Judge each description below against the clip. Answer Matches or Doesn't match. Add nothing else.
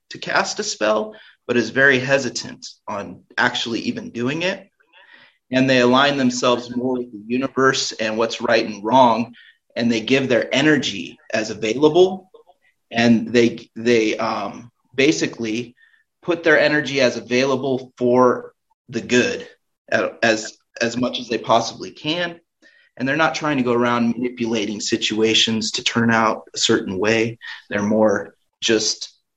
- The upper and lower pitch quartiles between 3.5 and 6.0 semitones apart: Doesn't match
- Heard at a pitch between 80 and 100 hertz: Doesn't match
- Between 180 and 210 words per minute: Doesn't match